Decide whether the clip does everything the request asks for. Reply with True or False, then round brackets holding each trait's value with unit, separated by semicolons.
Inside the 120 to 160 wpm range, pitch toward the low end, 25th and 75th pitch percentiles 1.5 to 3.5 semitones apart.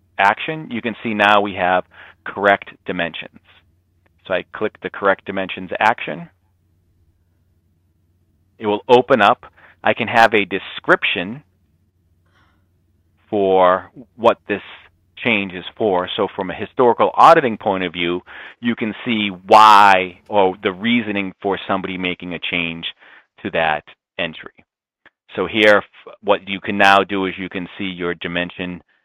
True (140 wpm; 95 Hz; 2.6 semitones)